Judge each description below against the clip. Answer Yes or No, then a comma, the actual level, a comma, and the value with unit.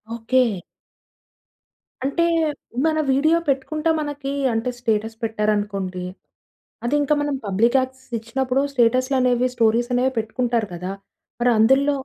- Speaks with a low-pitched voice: No, very high, 250 Hz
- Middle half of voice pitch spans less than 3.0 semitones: No, average, 3.4 semitones